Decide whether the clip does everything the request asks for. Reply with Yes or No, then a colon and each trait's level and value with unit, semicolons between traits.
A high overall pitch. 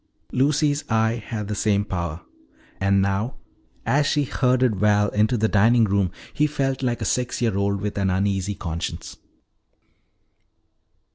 No: low, 105 Hz